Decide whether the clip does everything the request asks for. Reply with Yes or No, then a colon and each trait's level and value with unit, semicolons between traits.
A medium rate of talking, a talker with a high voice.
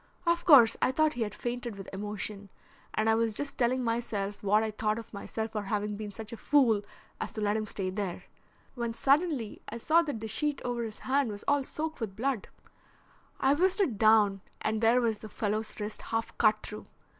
No: fast, 210 wpm; high, 225 Hz